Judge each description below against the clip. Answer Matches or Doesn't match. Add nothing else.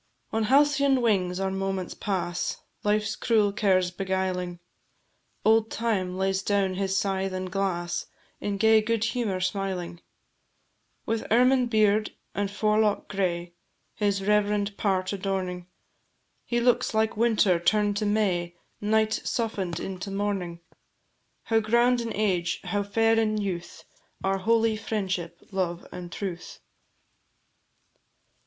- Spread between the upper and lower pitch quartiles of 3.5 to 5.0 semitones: Doesn't match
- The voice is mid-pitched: Doesn't match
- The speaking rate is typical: Doesn't match